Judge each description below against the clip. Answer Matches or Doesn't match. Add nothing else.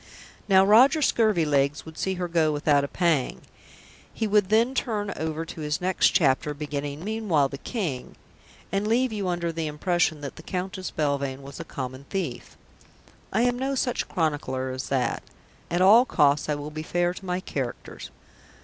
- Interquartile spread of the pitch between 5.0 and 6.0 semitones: Matches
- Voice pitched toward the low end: Doesn't match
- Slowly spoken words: Doesn't match